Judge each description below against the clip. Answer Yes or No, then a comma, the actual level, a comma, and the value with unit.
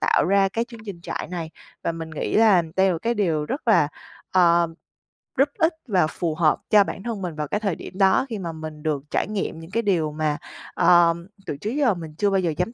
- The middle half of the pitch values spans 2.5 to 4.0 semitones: No, average, 4.4 semitones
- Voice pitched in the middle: Yes, medium, 180 Hz